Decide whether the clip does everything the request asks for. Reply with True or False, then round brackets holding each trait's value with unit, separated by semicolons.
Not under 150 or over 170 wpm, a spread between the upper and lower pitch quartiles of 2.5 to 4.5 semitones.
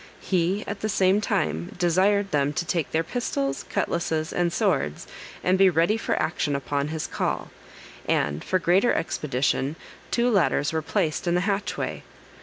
False (160 wpm; 4.9 semitones)